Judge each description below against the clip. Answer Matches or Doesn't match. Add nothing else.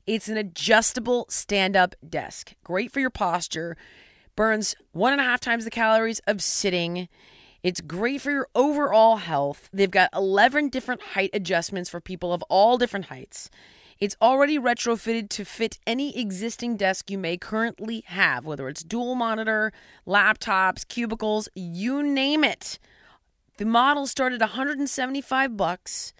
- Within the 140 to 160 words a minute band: Matches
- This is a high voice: Matches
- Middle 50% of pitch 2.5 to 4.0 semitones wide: Doesn't match